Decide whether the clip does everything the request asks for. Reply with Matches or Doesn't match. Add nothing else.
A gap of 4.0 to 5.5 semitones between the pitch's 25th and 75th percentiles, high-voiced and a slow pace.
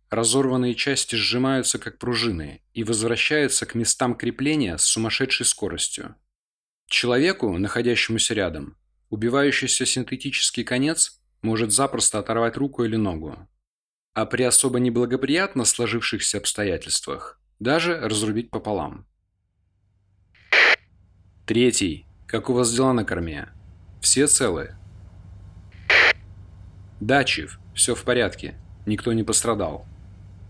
Doesn't match